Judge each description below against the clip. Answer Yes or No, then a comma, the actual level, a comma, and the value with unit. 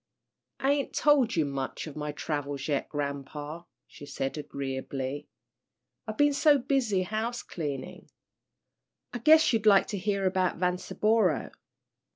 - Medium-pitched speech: Yes, medium, 180 Hz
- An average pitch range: No, wide, 7.8 semitones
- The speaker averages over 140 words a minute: No, slow, 135 wpm